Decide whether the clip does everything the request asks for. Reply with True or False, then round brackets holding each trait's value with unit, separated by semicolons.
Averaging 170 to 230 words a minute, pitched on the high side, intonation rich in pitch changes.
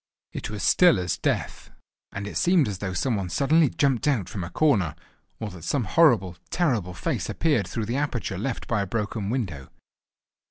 False (190 wpm; 110 Hz; 6.8 semitones)